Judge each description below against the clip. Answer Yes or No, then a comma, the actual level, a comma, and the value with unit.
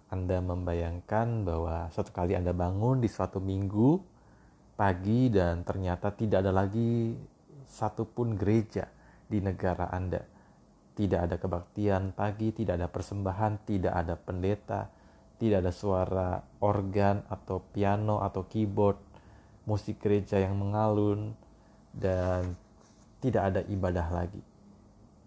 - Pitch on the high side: No, low, 100 Hz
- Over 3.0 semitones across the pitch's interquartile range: No, average, 2.7 semitones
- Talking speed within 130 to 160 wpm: No, average, 115 wpm